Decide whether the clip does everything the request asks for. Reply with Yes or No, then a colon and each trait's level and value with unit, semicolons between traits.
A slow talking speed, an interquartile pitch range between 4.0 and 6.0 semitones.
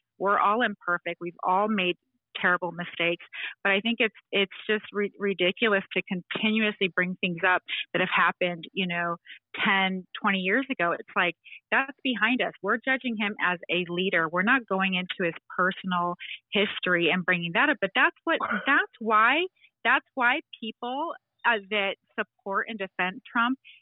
No: average, 165 wpm; average, 4.4 semitones